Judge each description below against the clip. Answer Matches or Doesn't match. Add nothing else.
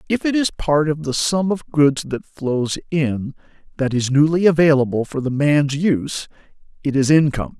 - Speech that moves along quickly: Doesn't match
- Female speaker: Doesn't match